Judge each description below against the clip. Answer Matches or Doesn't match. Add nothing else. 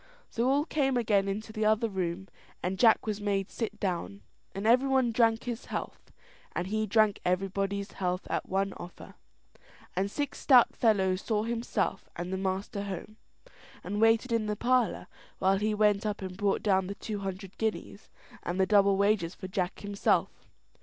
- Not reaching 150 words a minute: Doesn't match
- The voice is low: Doesn't match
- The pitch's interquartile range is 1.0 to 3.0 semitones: Matches